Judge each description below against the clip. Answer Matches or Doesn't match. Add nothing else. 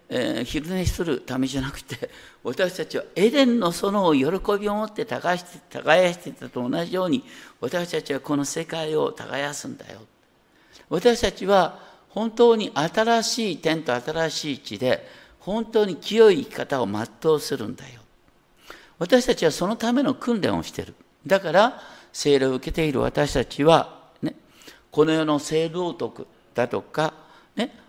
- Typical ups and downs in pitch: Doesn't match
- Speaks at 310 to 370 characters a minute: Doesn't match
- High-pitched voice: Doesn't match